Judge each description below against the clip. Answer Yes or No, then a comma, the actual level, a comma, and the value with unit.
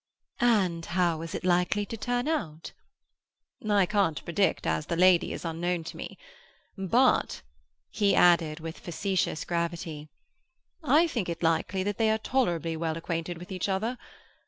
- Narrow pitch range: No, average, 3.8 semitones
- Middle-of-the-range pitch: Yes, medium, 180 Hz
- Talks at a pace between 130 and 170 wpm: Yes, average, 155 wpm